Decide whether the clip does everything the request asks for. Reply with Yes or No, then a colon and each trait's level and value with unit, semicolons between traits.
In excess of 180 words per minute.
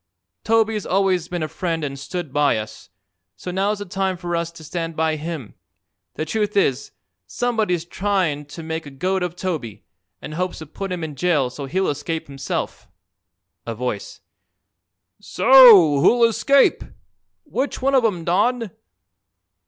No: average, 155 wpm